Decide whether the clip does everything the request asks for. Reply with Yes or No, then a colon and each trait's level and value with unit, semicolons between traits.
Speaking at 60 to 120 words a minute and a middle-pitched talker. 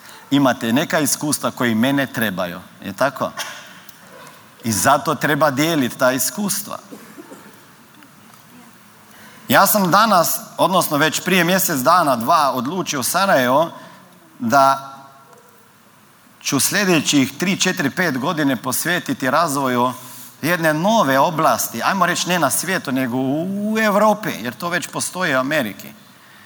Yes: average, 115 wpm; medium, 155 Hz